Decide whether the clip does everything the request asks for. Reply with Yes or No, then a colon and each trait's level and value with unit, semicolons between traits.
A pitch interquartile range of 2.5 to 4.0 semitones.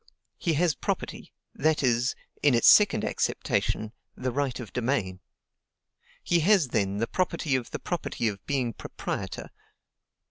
No: average, 5.3 semitones